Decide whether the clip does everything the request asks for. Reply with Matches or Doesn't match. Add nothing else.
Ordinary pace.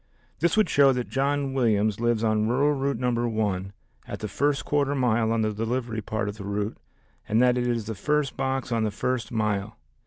Doesn't match